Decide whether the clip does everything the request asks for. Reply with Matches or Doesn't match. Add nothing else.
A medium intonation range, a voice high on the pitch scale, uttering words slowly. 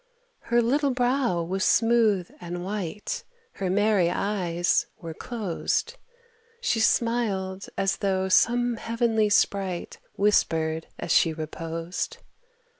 Matches